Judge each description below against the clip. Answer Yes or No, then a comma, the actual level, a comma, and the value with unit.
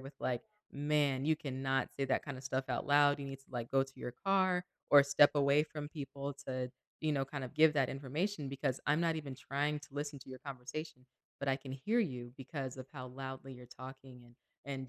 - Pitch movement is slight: Yes, narrow, 2.0 semitones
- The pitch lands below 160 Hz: Yes, low, 135 Hz